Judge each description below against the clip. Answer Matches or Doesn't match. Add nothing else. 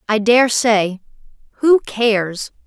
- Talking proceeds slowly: Matches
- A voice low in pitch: Doesn't match